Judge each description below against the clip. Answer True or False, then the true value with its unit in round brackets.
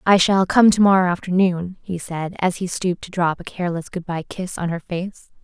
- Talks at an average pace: False (220 wpm)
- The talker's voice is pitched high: False (180 Hz)